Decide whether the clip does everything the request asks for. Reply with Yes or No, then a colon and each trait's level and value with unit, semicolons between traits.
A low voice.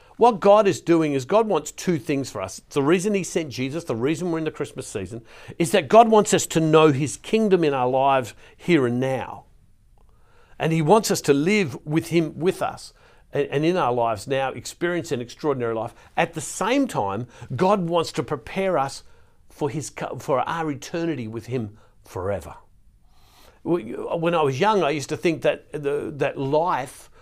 No: medium, 155 Hz